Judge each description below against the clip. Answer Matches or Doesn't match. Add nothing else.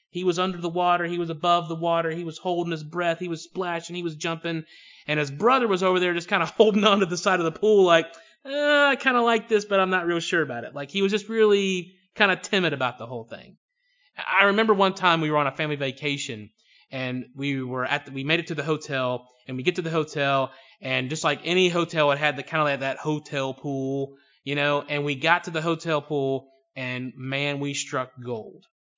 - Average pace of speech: Doesn't match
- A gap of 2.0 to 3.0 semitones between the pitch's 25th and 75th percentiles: Doesn't match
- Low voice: Doesn't match